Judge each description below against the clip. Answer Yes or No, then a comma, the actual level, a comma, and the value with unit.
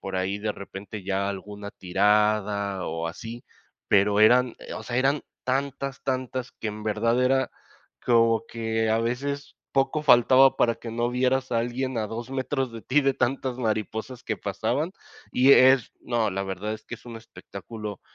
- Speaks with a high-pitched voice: No, low, 115 Hz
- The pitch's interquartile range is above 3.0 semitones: Yes, average, 3.6 semitones